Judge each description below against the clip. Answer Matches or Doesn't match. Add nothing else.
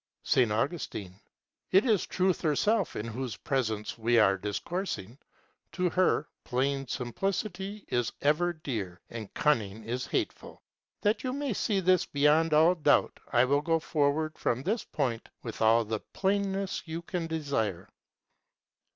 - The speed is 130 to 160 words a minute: Matches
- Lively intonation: Matches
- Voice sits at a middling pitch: Matches